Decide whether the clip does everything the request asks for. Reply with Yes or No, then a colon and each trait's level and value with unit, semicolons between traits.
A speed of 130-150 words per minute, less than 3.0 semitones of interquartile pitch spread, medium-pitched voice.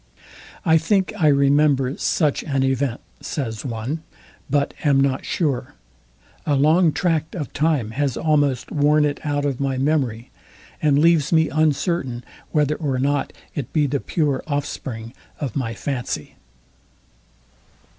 Yes: slow, 135 wpm; narrow, 2.5 semitones; medium, 145 Hz